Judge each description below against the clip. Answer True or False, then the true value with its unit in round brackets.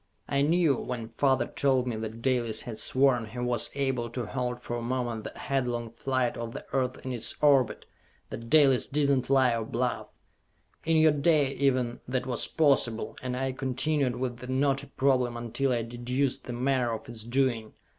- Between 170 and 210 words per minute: True (185 wpm)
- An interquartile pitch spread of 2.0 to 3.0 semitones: True (2.4 semitones)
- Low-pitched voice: True (125 Hz)